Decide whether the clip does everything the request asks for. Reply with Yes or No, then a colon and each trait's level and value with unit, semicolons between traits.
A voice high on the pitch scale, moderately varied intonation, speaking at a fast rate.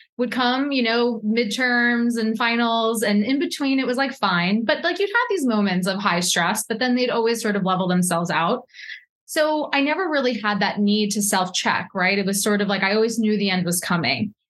Yes: high, 225 Hz; average, 3.9 semitones; fast, 225 wpm